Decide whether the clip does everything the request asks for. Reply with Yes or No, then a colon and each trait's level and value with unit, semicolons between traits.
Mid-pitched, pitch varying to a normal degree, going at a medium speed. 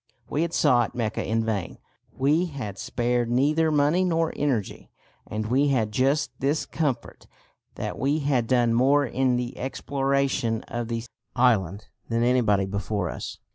No: low, 125 Hz; average, 4.0 semitones; average, 150 wpm